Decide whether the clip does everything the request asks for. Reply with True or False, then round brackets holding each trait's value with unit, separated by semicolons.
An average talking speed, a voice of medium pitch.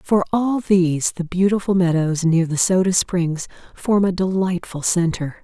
True (155 wpm; 180 Hz)